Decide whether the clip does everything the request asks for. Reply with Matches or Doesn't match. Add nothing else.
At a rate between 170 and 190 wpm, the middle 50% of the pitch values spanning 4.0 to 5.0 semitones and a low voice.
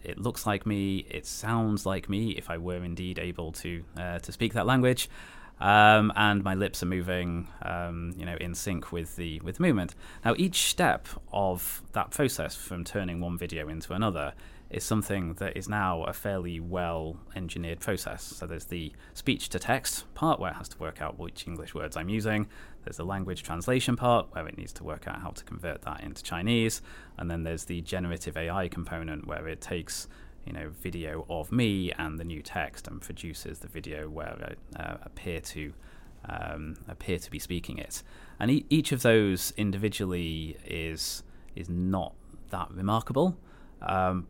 Doesn't match